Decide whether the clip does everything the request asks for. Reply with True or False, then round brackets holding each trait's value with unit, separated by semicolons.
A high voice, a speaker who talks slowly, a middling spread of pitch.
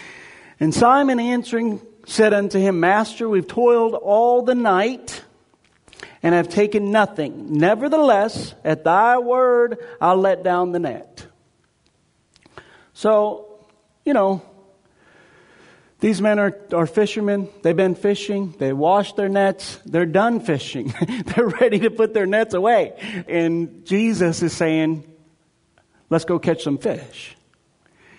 True (200 Hz; 125 wpm; 4.5 semitones)